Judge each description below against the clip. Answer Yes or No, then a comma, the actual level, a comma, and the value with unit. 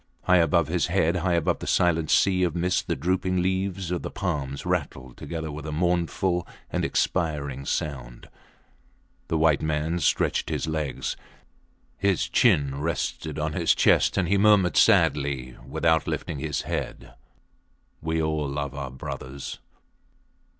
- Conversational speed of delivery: Yes, average, 145 wpm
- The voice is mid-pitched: No, very low, 80 Hz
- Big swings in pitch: No, average, 3.6 semitones